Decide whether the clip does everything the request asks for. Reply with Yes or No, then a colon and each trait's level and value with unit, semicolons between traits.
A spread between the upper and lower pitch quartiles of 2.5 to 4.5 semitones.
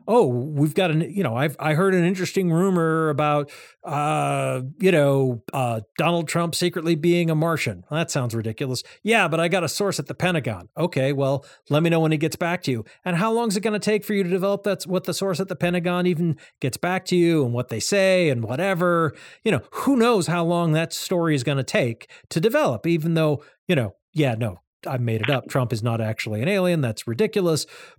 No: average, 5.0 semitones